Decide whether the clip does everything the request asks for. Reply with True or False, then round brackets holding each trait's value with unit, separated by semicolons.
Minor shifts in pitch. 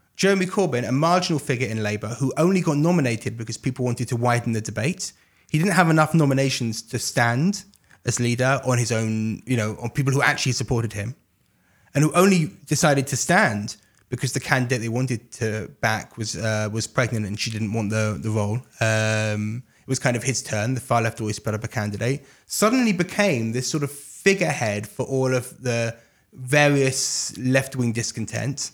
False (4.2 semitones)